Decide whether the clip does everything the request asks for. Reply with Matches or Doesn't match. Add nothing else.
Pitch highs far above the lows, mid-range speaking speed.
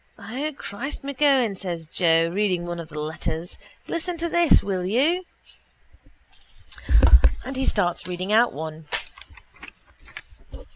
Doesn't match